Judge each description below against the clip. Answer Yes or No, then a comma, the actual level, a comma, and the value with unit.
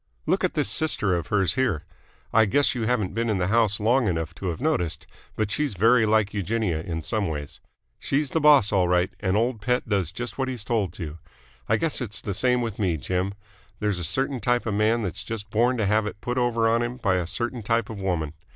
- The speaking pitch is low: Yes, low, 105 Hz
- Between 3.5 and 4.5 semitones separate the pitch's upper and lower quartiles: Yes, average, 4.2 semitones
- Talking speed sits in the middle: No, fast, 235 wpm